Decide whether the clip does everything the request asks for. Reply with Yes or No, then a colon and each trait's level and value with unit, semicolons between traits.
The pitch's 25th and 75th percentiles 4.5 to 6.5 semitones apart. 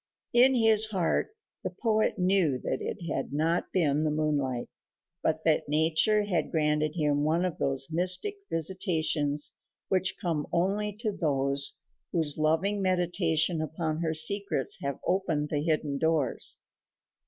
No: average, 3.9 semitones